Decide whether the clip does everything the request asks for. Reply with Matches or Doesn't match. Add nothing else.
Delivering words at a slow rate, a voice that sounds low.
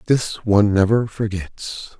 Matches